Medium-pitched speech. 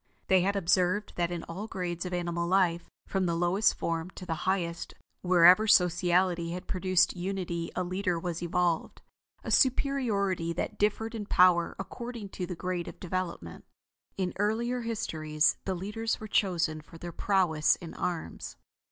Yes: medium, 180 Hz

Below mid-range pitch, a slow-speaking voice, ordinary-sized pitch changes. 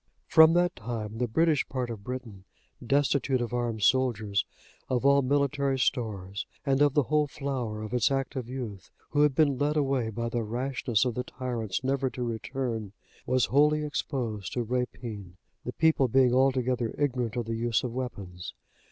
No: low, 125 Hz; average, 170 wpm; average, 3.3 semitones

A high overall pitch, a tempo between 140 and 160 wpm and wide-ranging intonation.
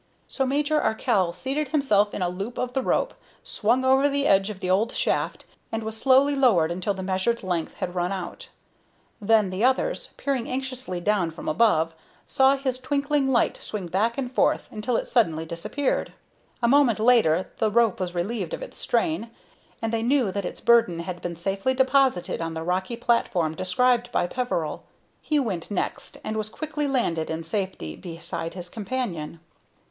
No: high, 220 Hz; average, 180 wpm; wide, 6.4 semitones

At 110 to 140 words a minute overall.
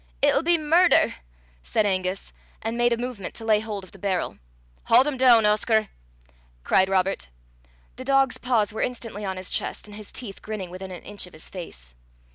No: average, 190 wpm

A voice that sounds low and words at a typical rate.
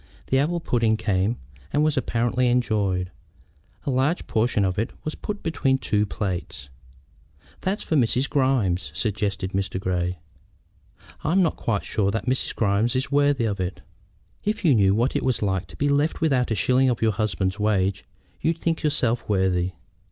Yes: low, 115 Hz; average, 170 wpm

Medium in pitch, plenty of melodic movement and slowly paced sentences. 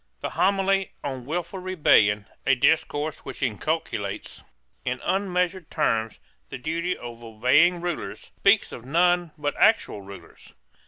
Yes: medium, 155 Hz; wide, 6.6 semitones; slow, 125 wpm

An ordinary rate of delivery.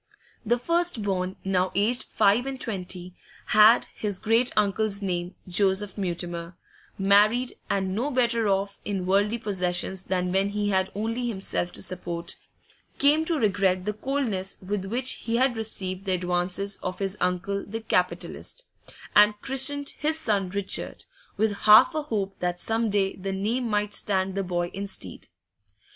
Yes: average, 155 wpm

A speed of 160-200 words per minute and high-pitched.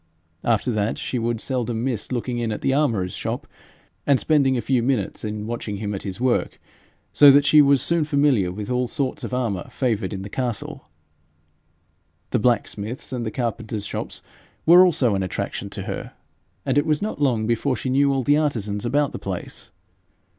No: average, 190 wpm; low, 120 Hz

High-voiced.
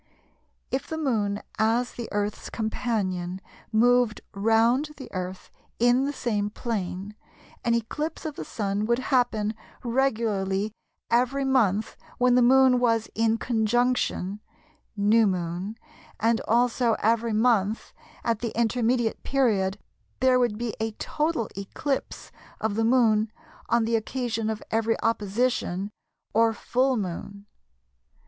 Yes: high, 225 Hz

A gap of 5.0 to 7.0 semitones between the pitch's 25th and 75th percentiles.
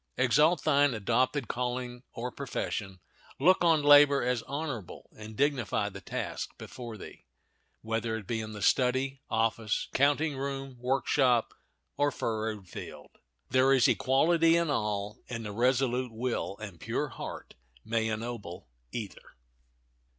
No: average, 3.8 semitones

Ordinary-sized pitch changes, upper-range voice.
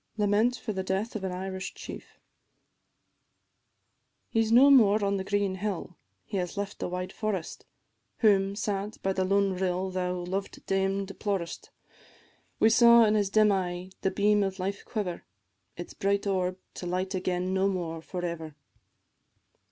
No: narrow, 1.9 semitones; high, 195 Hz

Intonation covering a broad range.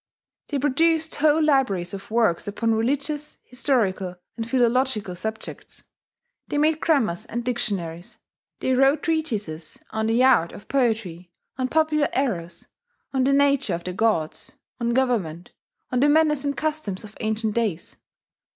Yes: wide, 6.0 semitones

